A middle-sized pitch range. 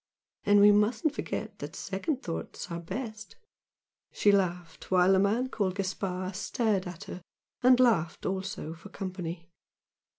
Yes: average, 3.0 semitones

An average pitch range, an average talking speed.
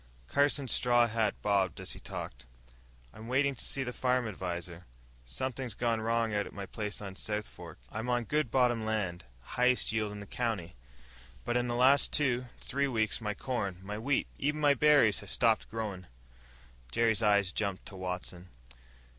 Yes: average, 3.6 semitones; average, 180 wpm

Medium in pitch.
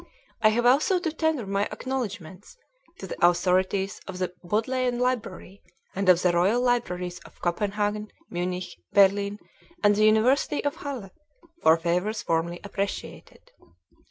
No: high, 200 Hz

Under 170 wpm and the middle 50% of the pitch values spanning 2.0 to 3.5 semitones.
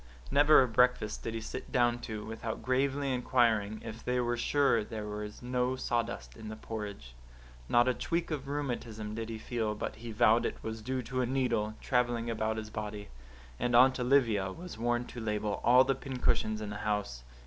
No: average, 190 wpm; average, 2.8 semitones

